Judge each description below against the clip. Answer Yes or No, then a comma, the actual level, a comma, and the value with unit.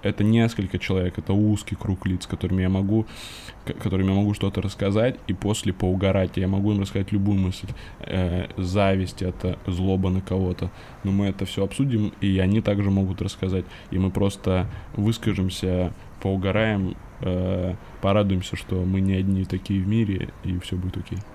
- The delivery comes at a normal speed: No, fast, 165 wpm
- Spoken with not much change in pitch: Yes, narrow, 1.8 semitones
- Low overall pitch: Yes, very low, 95 Hz